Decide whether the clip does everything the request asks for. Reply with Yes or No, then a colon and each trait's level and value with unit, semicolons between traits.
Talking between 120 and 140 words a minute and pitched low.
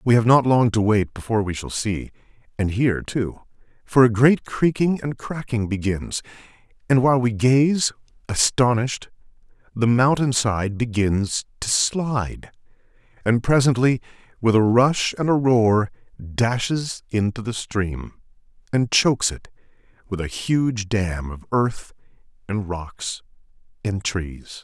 Yes: slow, 135 wpm; low, 115 Hz